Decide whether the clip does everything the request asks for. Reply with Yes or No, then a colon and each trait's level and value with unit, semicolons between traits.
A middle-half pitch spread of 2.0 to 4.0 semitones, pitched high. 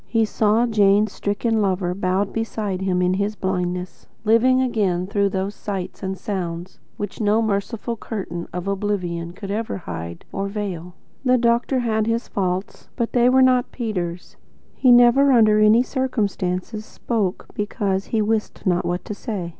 Yes: average, 3.5 semitones; high, 205 Hz